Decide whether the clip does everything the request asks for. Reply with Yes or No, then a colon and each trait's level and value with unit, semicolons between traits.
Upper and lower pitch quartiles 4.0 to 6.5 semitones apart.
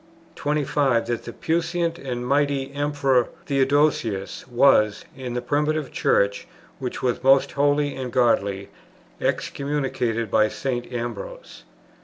No: average, 3.2 semitones